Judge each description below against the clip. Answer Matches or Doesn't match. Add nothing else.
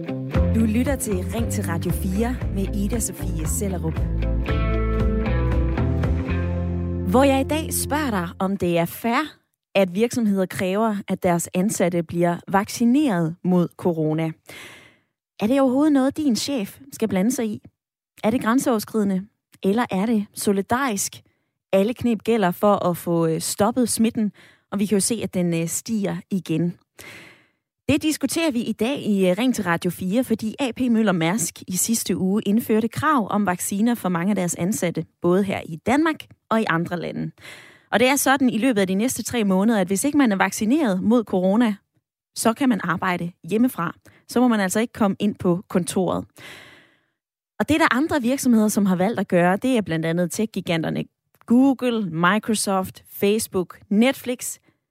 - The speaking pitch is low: Doesn't match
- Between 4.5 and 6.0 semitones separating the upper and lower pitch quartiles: Matches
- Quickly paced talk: Doesn't match